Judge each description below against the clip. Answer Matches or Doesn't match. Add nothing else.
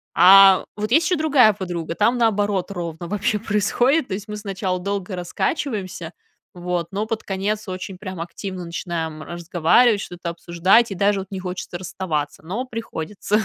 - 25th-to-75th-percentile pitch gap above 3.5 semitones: Doesn't match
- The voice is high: Matches